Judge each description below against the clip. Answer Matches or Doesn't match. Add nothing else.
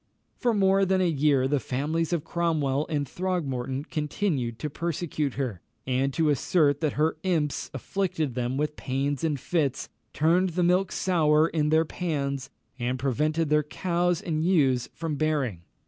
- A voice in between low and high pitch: Matches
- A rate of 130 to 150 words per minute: Doesn't match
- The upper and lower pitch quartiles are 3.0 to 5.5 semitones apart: Matches